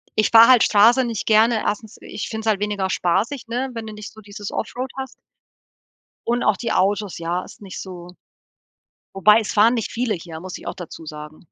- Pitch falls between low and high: No, high, 210 Hz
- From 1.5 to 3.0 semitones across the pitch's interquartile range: No, average, 3.5 semitones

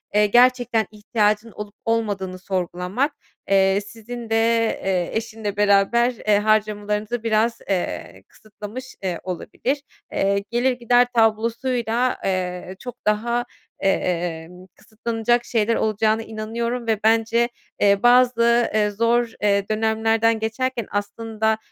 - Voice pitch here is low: No, high, 220 Hz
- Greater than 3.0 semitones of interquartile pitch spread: No, narrow, 2.4 semitones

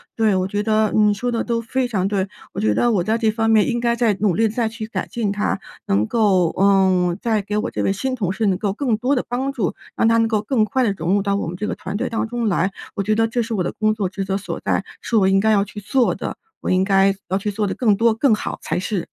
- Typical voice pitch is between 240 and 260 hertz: No, high, 215 Hz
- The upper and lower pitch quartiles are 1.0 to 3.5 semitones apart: Yes, average, 2.8 semitones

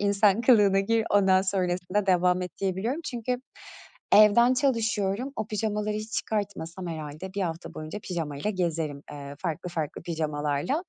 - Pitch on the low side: No, high, 190 Hz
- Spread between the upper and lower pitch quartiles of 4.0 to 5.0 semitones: Yes, average, 4.3 semitones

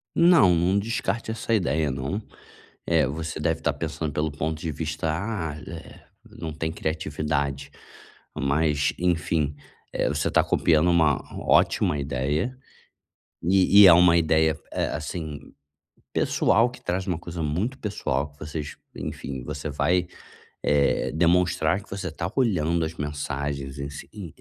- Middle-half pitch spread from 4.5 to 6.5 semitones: No, average, 3.5 semitones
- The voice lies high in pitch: No, very low, 80 Hz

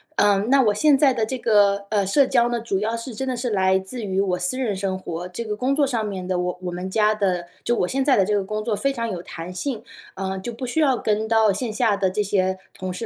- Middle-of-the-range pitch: No, high, 210 Hz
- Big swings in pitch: No, average, 4.1 semitones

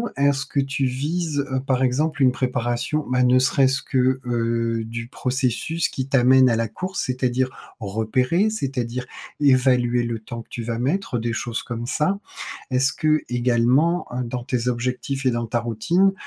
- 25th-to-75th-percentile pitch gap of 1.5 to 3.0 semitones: Yes, narrow, 2.4 semitones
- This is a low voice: Yes, low, 125 Hz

